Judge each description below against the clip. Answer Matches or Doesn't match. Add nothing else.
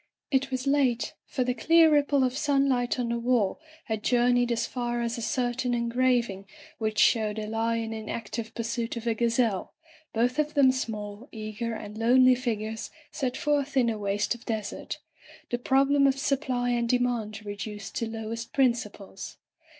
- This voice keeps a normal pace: Matches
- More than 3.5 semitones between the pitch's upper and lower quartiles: Doesn't match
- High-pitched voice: Matches